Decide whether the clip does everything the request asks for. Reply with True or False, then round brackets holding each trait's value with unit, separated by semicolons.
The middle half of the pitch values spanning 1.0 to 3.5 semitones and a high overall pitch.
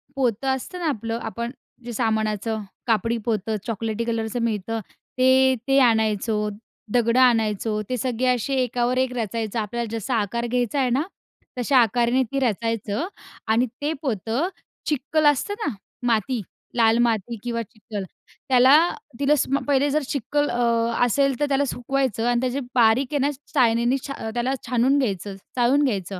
True (2.8 semitones; 235 Hz)